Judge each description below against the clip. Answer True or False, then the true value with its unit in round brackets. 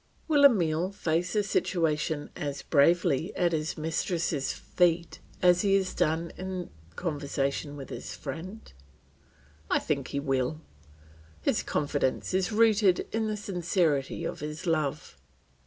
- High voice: False (165 Hz)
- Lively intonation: False (4.1 semitones)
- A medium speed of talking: False (130 wpm)